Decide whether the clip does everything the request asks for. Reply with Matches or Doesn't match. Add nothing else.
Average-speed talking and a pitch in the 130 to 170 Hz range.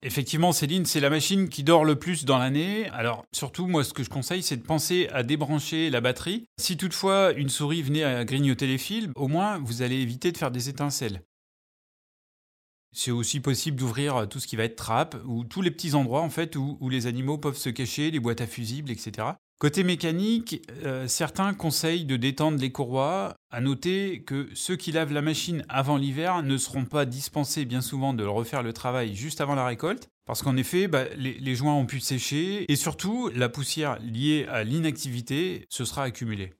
Matches